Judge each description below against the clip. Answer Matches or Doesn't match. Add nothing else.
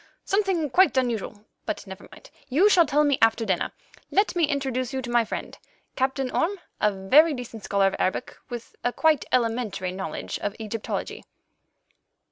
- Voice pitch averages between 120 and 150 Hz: Doesn't match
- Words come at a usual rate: Matches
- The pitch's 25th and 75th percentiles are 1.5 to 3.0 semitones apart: Doesn't match